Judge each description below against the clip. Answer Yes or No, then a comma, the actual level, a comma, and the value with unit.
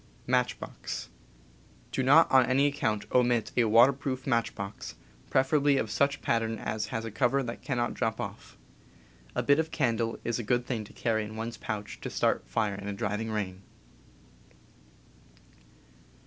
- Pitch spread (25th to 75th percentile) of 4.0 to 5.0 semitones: No, average, 3.3 semitones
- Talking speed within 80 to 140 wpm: No, average, 160 wpm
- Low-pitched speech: Yes, low, 115 Hz